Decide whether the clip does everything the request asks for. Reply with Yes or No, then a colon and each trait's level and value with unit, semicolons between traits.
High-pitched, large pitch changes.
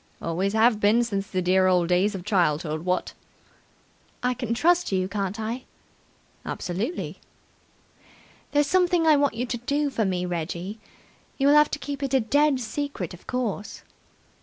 Yes: high, 220 Hz; wide, 7.0 semitones